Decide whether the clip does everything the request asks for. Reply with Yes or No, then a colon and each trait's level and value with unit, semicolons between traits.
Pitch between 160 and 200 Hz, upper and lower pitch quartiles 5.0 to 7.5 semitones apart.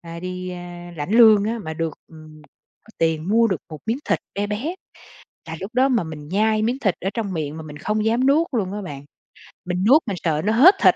Yes: high, 190 Hz; wide, 5.5 semitones